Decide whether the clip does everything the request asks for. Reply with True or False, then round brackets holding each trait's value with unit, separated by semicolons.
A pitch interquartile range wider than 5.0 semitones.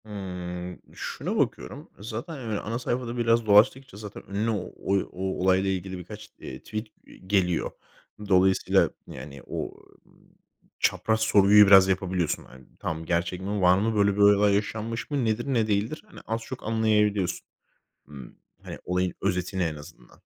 False (3.4 semitones)